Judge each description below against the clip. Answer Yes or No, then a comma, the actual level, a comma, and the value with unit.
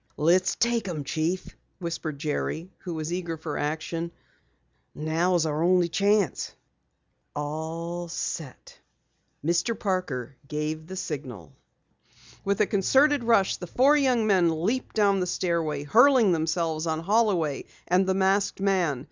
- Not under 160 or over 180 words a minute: No, slow, 135 wpm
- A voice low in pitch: No, medium, 175 Hz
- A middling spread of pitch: Yes, average, 3.8 semitones